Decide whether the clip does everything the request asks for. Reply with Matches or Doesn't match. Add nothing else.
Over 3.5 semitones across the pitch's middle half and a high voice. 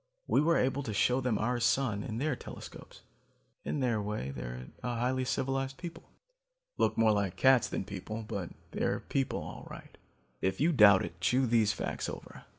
Doesn't match